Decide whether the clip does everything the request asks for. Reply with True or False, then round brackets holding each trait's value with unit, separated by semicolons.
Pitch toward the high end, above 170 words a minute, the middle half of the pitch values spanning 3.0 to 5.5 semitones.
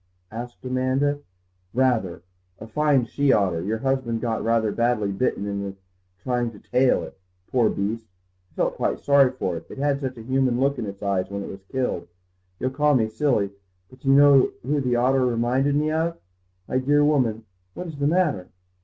False (125 Hz; 190 wpm; 4.0 semitones)